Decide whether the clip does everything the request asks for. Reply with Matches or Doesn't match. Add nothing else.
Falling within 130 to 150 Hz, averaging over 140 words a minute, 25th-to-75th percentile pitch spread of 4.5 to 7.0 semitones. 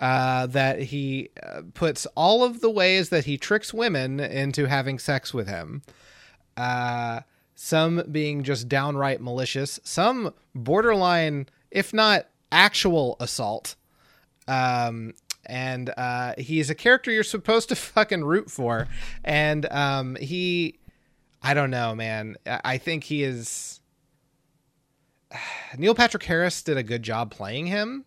Doesn't match